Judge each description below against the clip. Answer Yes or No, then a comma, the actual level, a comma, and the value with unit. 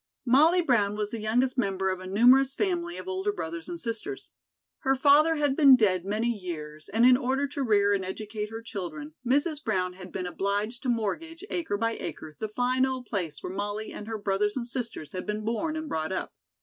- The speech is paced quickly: Yes, fast, 210 wpm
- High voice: Yes, high, 225 Hz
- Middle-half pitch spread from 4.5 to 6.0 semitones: Yes, wide, 5.4 semitones